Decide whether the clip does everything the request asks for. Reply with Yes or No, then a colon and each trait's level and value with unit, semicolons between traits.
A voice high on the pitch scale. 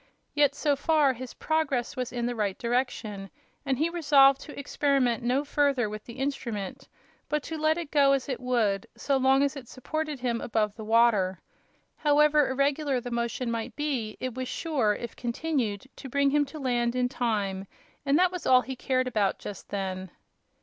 Yes: very high, 255 Hz